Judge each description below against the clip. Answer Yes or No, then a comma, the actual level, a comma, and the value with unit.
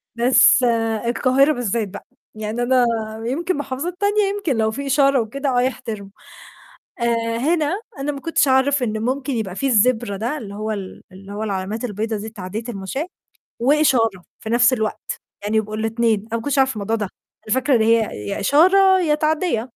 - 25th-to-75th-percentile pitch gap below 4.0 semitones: No, average, 4.3 semitones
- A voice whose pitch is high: Yes, high, 235 Hz